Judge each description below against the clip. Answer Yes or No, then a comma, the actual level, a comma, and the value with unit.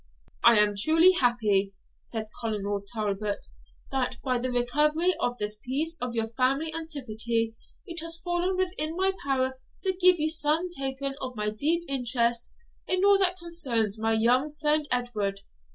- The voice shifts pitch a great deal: Yes, wide, 6.3 semitones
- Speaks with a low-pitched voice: No, very high, 260 Hz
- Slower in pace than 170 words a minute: Yes, average, 150 wpm